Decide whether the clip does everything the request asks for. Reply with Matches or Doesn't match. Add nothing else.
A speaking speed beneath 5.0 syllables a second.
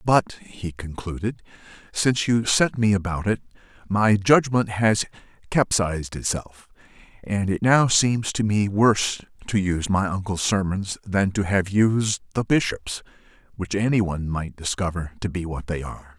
Matches